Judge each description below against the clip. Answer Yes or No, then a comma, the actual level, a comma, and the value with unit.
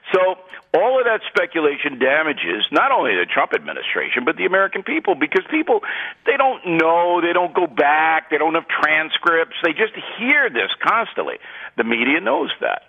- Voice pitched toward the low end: No, medium, 180 Hz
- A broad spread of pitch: Yes, wide, 8.5 semitones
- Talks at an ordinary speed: Yes, average, 170 wpm